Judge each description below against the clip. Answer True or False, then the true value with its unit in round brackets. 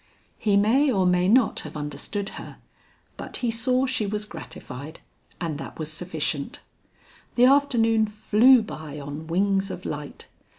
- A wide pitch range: True (6.3 semitones)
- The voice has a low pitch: False (200 Hz)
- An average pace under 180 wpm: True (145 wpm)